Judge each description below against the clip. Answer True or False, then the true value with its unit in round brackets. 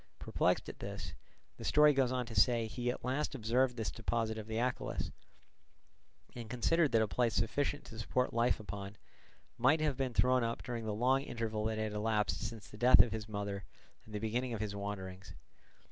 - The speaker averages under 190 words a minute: False (195 wpm)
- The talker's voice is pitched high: False (115 Hz)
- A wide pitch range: False (2.9 semitones)